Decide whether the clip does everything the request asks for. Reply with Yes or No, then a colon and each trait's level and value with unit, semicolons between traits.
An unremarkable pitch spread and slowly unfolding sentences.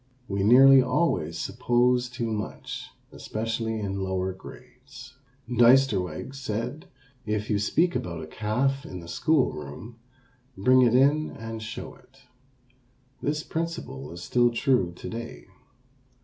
Yes: average, 4.4 semitones; slow, 130 wpm